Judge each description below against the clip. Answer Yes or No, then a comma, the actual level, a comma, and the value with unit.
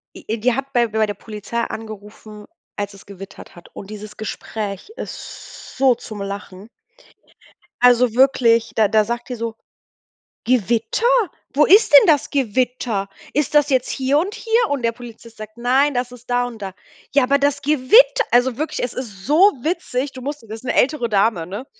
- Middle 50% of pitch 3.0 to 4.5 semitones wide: Yes, average, 4.1 semitones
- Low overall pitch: No, high, 240 Hz